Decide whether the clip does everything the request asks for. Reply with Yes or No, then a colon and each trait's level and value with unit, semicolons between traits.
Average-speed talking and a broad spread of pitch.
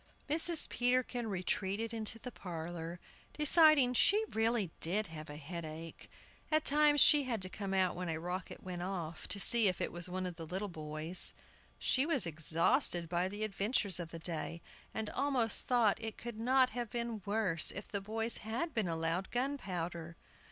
Yes: average, 175 wpm; wide, 5.8 semitones